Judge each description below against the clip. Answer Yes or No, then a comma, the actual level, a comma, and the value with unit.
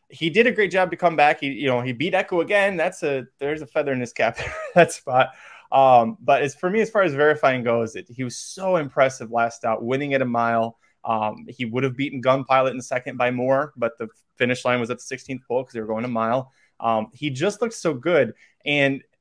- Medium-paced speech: No, fast, 245 wpm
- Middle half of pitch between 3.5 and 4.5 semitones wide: Yes, average, 3.8 semitones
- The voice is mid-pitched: No, low, 130 Hz